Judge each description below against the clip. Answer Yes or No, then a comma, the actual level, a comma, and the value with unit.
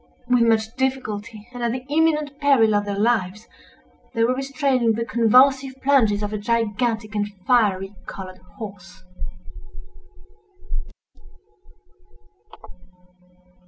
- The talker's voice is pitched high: Yes, high, 230 Hz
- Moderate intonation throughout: Yes, average, 3.9 semitones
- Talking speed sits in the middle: No, slow, 105 wpm